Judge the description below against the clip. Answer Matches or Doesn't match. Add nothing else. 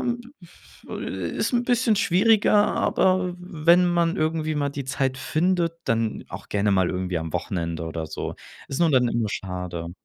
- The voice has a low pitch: Doesn't match